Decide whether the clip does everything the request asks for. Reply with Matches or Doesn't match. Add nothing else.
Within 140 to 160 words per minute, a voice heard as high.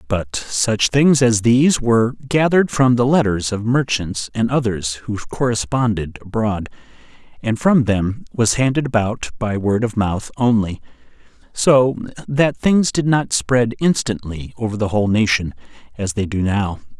Doesn't match